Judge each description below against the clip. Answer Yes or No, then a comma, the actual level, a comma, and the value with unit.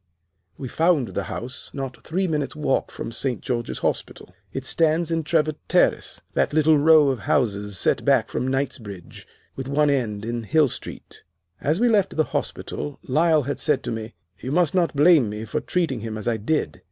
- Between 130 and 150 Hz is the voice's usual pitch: Yes, medium, 140 Hz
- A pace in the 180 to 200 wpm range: Yes, average, 190 wpm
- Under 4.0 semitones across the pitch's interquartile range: No, average, 5.1 semitones